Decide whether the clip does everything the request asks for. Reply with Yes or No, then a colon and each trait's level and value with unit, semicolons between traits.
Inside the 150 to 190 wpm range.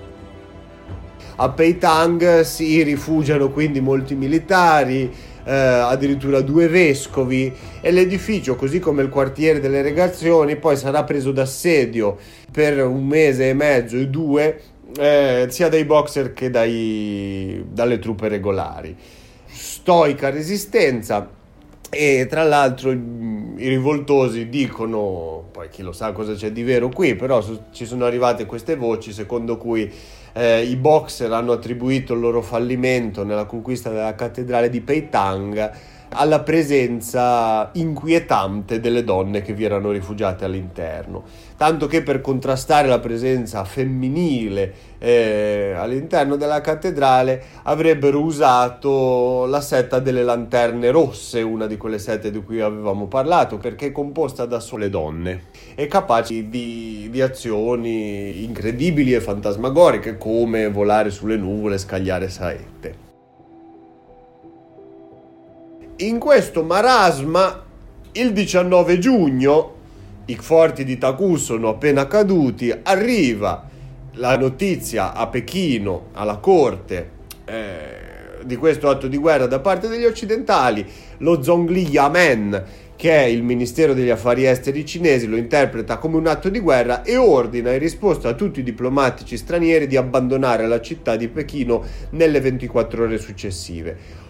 No: average, 130 wpm